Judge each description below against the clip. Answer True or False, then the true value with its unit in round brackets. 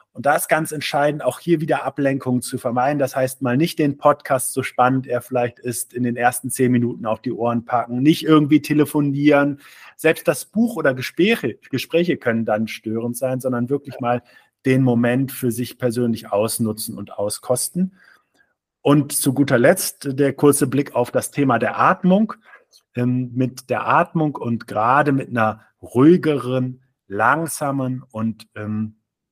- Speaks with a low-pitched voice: True (130 Hz)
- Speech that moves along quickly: False (160 wpm)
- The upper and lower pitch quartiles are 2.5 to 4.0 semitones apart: True (3.2 semitones)